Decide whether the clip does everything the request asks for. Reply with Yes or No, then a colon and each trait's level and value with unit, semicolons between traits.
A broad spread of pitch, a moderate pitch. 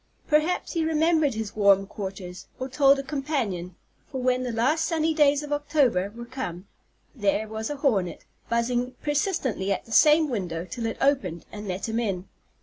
No: wide, 6.5 semitones; very high, 250 Hz